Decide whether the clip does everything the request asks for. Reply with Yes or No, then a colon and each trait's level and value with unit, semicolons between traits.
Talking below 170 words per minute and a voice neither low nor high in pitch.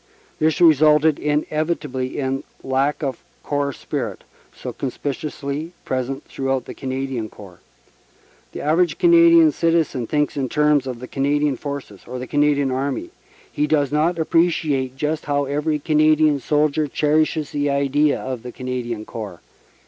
Yes: average, 145 wpm; medium, 145 Hz